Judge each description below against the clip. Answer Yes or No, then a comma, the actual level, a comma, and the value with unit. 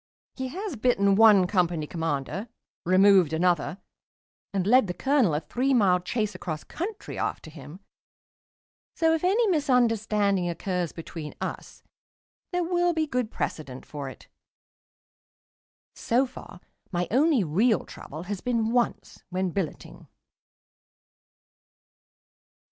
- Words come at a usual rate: No, slow, 120 wpm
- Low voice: No, high, 200 Hz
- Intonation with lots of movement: Yes, wide, 6.4 semitones